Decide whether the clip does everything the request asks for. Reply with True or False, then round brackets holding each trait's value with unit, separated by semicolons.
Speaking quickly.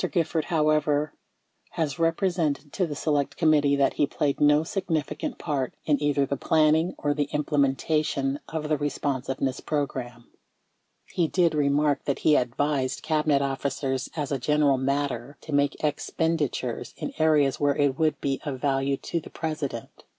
False (155 wpm)